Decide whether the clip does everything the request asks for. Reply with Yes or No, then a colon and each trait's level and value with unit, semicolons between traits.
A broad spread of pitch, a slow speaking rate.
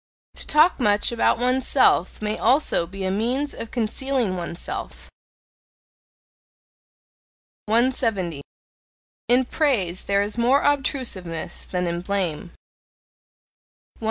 Yes: wide, 5.8 semitones; slow, 100 wpm